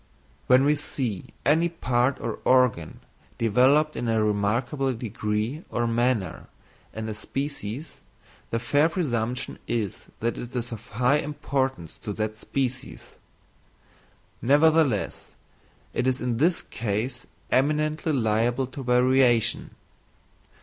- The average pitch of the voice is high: No, low, 125 Hz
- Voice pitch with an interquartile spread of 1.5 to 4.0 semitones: Yes, average, 3.7 semitones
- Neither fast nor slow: No, slow, 115 wpm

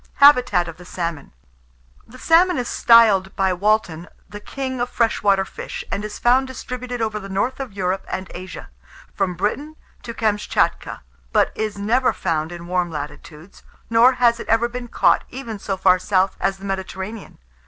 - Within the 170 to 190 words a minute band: Yes, average, 175 wpm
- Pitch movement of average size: Yes, average, 4.5 semitones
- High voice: Yes, high, 205 Hz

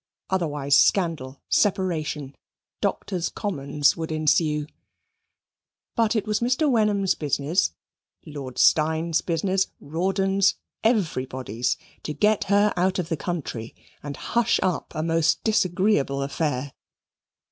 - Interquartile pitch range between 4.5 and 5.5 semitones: Yes, average, 5.1 semitones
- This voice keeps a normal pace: No, slow, 110 wpm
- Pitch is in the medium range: Yes, medium, 165 Hz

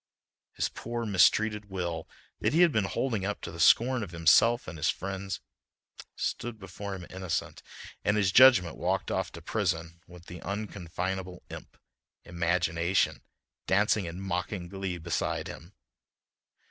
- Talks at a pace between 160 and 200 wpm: No, average, 145 wpm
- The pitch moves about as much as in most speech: Yes, average, 3.2 semitones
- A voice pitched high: No, very low, 95 Hz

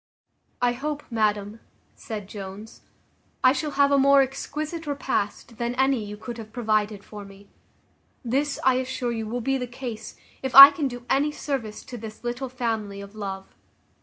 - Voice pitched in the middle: No, high, 240 Hz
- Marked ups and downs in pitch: No, average, 4.0 semitones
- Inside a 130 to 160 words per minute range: No, average, 170 wpm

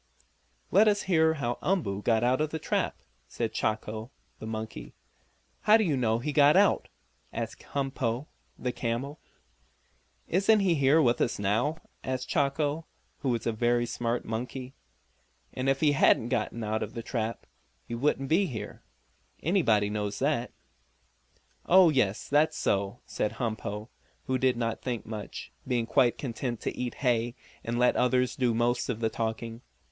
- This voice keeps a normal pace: Yes, average, 160 wpm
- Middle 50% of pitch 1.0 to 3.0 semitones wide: No, average, 4.1 semitones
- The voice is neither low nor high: No, low, 125 Hz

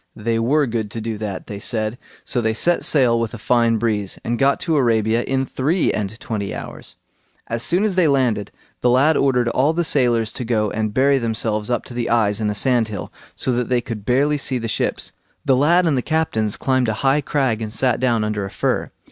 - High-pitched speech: No, low, 120 Hz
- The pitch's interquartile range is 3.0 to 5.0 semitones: Yes, average, 3.5 semitones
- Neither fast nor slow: No, fast, 225 wpm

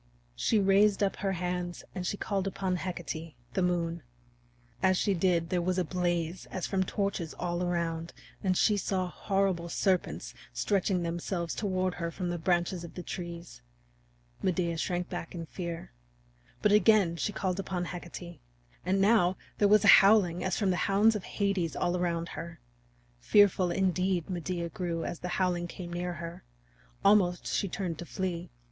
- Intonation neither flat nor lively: No, narrow, 2.0 semitones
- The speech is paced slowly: No, average, 165 wpm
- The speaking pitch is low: No, medium, 180 Hz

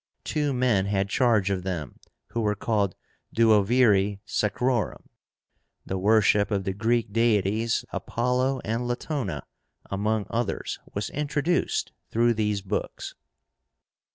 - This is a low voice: Yes, low, 110 Hz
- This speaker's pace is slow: Yes, slow, 115 wpm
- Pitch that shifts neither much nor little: Yes, average, 3.4 semitones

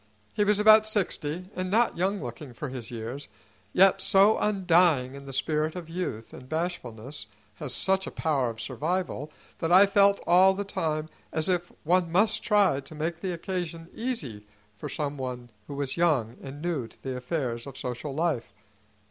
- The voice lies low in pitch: No, medium, 160 Hz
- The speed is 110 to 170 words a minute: No, average, 180 wpm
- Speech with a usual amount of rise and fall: No, wide, 5.7 semitones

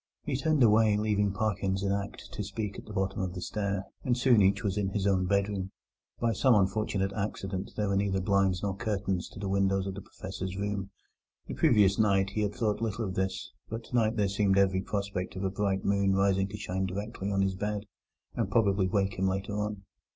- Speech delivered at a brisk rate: Yes, fast, 215 wpm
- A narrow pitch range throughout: Yes, narrow, 1.5 semitones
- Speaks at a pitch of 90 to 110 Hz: Yes, low, 100 Hz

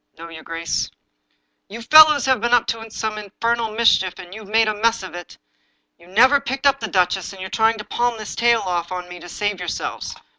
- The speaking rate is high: Yes, fast, 235 wpm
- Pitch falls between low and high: No, high, 215 Hz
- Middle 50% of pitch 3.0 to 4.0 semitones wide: No, average, 4.5 semitones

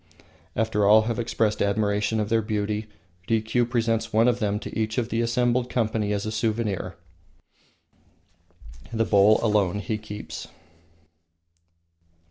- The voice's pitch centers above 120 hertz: No, low, 110 Hz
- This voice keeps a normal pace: No, slow, 130 wpm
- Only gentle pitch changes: Yes, narrow, 1.6 semitones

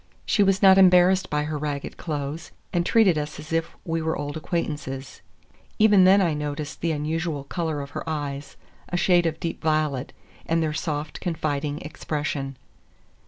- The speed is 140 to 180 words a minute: Yes, average, 160 wpm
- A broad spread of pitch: No, average, 2.8 semitones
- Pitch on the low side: No, medium, 155 Hz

